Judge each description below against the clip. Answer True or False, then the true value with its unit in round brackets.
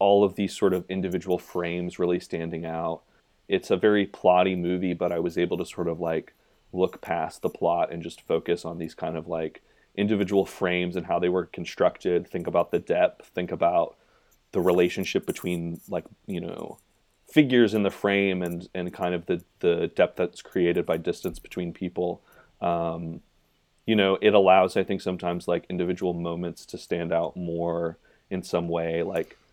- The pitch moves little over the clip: True (1.7 semitones)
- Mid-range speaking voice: False (90 Hz)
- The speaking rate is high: False (185 wpm)